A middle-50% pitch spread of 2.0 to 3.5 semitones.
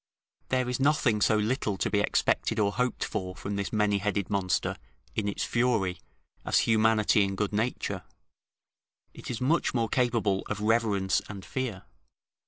Yes: average, 2.8 semitones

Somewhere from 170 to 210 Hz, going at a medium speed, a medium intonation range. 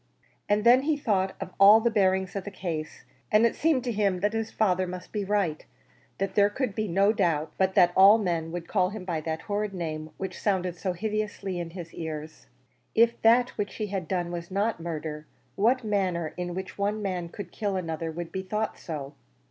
No: high, 190 Hz; fast, 210 wpm; average, 3.5 semitones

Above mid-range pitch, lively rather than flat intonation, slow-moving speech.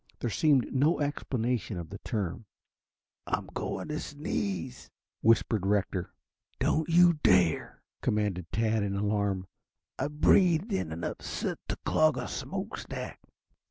No: low, 115 Hz; wide, 7.2 semitones; slow, 130 wpm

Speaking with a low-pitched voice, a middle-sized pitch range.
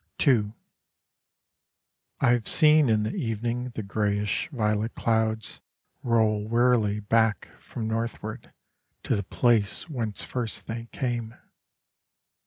No: low, 115 Hz; narrow, 2.2 semitones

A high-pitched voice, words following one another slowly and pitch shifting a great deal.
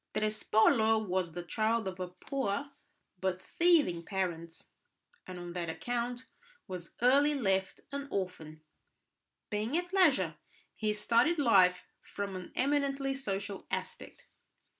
Yes: high, 210 Hz; slow, 120 wpm; wide, 6.7 semitones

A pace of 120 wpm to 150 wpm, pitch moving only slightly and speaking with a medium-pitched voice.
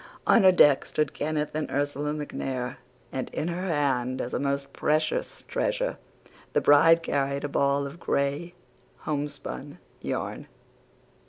Yes: average, 140 wpm; narrow, 2.0 semitones; medium, 145 Hz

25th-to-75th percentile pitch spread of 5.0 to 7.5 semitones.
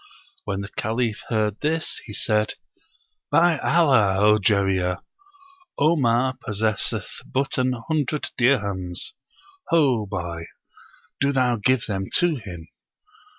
Yes: wide, 5.6 semitones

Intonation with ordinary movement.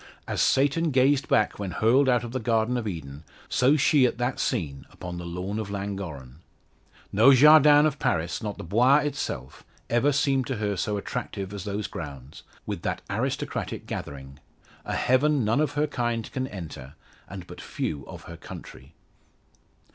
No: wide, 7.0 semitones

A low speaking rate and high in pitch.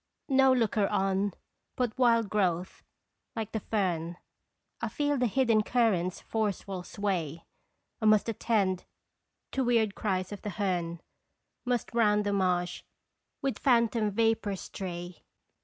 Yes: slow, 125 wpm; high, 210 Hz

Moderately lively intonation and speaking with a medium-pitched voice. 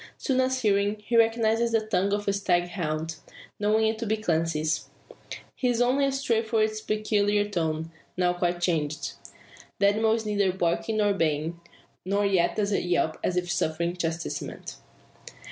No: average, 4.2 semitones; high, 200 Hz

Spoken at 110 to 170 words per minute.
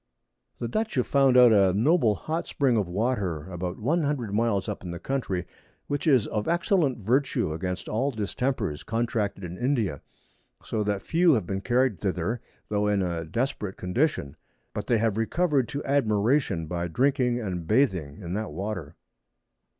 Yes: average, 165 wpm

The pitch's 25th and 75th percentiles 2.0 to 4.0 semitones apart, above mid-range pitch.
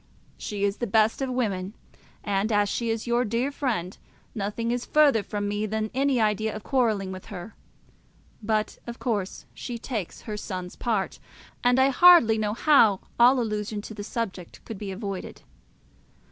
Yes: average, 2.8 semitones; high, 215 Hz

